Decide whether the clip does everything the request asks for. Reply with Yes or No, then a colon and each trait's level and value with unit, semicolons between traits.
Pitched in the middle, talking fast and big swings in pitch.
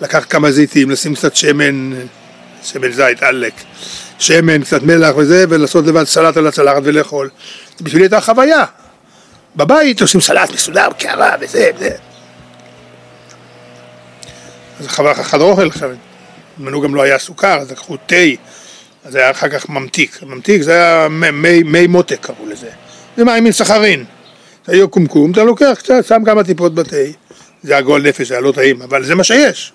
Yes: medium, 155 Hz; fast, 170 wpm; wide, 6.8 semitones